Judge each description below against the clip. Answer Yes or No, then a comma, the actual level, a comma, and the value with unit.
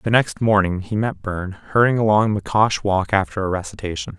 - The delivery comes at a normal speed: Yes, average, 185 wpm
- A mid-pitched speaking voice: No, low, 100 Hz